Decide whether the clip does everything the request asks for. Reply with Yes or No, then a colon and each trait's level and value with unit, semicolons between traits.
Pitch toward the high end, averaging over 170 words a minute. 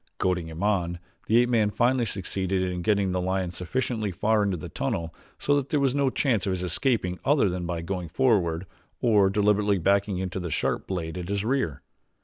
No: very low, 95 Hz; average, 200 wpm